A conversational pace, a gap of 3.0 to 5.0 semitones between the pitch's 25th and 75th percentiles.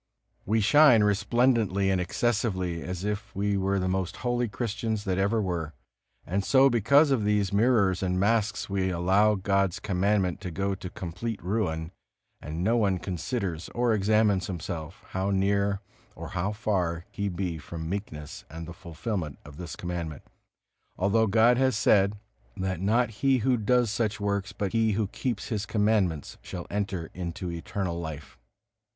Yes: average, 160 wpm; average, 3.3 semitones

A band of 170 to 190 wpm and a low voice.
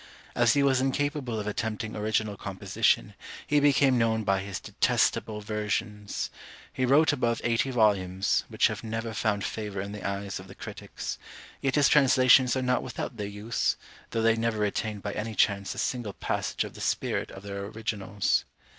Yes: average, 175 wpm; low, 110 Hz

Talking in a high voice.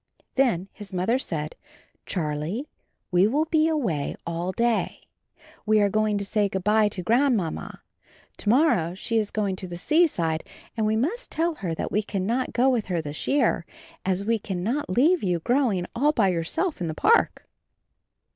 Yes: high, 210 Hz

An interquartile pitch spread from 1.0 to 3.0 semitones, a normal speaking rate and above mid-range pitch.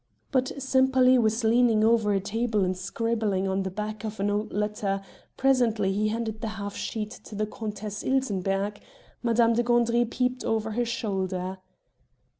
Yes: narrow, 2.6 semitones; average, 160 wpm; high, 220 Hz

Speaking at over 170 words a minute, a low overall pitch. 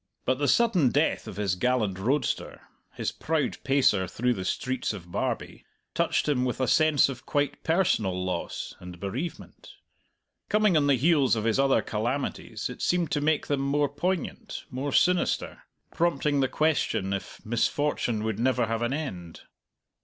No: average, 160 wpm; low, 130 Hz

